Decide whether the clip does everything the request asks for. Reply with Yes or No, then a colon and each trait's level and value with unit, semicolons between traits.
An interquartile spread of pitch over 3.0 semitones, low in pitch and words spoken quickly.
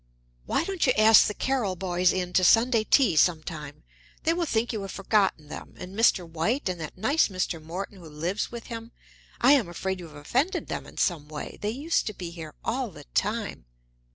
No: wide, 5.4 semitones; high, 195 Hz; fast, 210 wpm